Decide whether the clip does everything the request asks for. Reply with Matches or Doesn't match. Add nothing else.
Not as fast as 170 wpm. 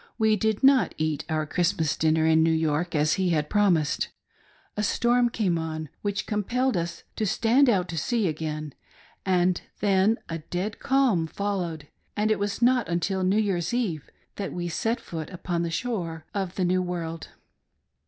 Doesn't match